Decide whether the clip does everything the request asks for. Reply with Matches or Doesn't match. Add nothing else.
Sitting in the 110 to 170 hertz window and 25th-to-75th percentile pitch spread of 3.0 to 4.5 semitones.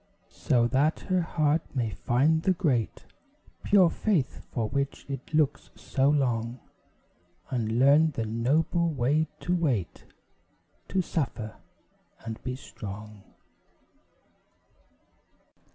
Doesn't match